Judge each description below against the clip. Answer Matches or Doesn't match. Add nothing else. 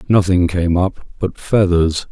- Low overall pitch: Matches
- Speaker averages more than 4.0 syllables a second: Doesn't match